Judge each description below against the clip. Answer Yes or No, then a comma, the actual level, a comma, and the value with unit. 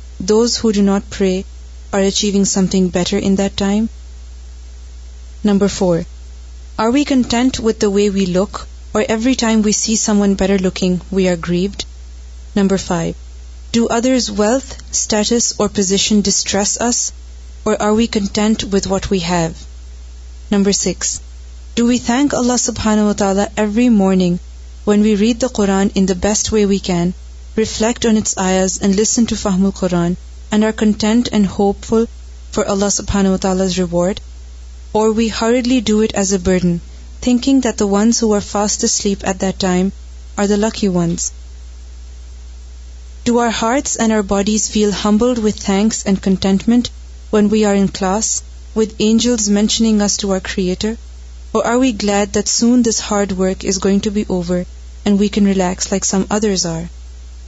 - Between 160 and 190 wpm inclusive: No, average, 140 wpm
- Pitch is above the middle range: Yes, high, 200 Hz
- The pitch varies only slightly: No, average, 4.0 semitones